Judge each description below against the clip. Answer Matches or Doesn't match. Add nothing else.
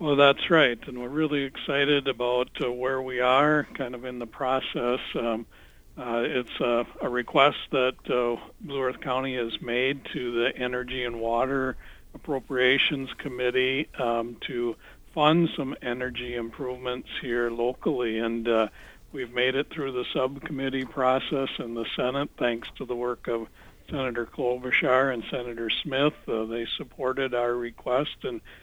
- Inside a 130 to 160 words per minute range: Matches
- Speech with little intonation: Matches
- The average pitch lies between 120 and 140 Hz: Matches